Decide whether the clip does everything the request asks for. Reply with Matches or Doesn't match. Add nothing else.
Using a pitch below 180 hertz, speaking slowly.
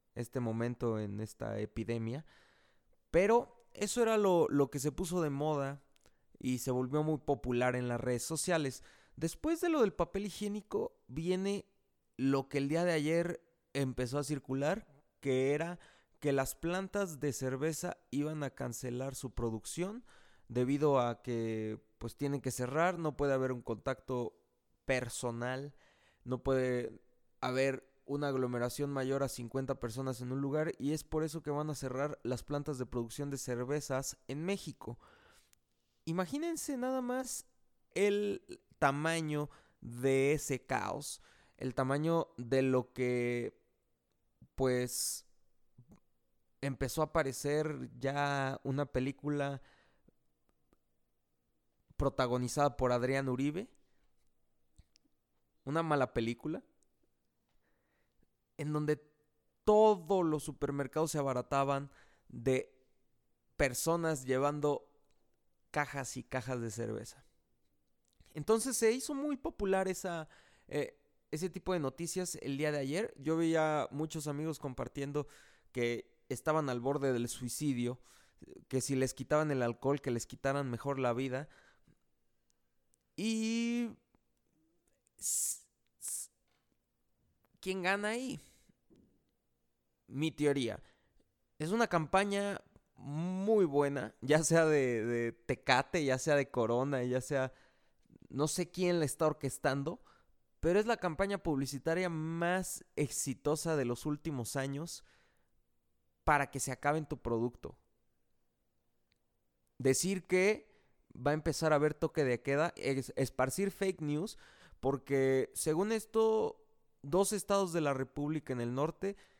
Matches